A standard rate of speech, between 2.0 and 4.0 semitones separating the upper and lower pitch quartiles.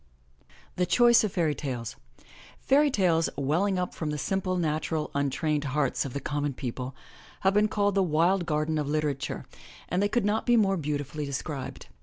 No: average, 185 wpm; average, 5.1 semitones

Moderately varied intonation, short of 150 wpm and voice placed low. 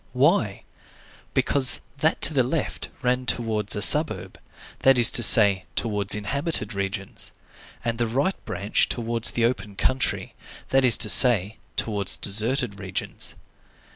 Yes: average, 4.0 semitones; average, 140 wpm; low, 115 Hz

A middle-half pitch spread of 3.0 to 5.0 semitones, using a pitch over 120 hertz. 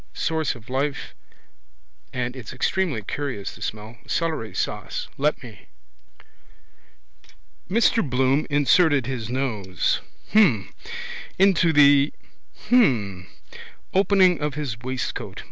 No: wide, 5.4 semitones; low, 135 Hz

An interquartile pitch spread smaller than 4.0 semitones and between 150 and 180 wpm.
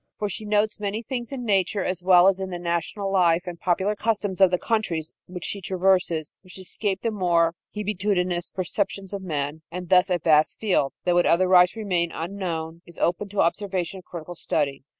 No: average, 2.7 semitones; average, 190 wpm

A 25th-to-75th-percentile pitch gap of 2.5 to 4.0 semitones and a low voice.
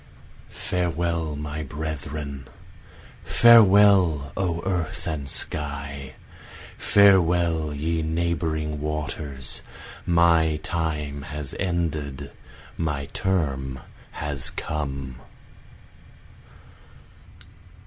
Yes: average, 2.9 semitones; very low, 75 Hz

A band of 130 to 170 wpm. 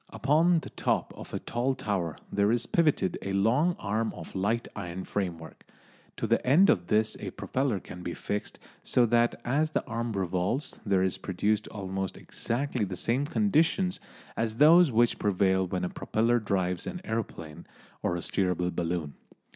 Yes: average, 165 wpm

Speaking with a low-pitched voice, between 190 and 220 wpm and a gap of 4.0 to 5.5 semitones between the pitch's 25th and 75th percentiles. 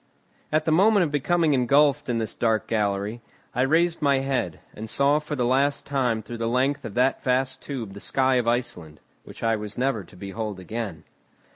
Yes: low, 125 Hz; average, 195 wpm; average, 4.3 semitones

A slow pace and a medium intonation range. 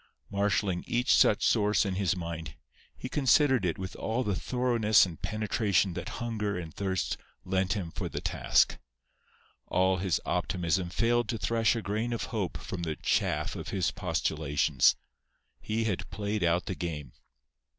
No: average, 160 wpm; average, 3.9 semitones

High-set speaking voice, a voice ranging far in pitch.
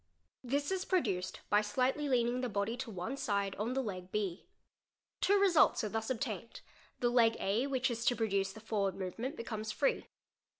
No: high, 230 Hz; average, 4.3 semitones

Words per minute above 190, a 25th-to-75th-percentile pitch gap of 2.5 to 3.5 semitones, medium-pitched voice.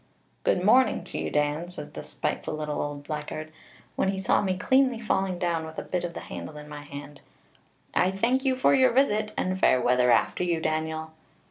No: fast, 205 wpm; average, 5.0 semitones; medium, 175 Hz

